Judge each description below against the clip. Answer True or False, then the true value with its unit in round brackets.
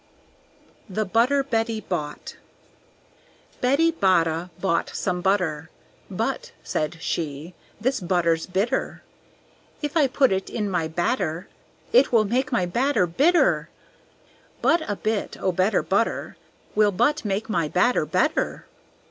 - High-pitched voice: True (195 Hz)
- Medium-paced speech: False (125 wpm)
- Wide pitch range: True (6.2 semitones)